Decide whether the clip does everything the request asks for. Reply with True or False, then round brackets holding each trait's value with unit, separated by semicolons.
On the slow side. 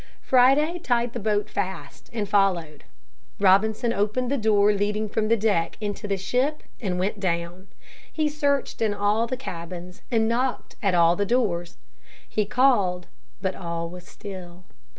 False (155 wpm)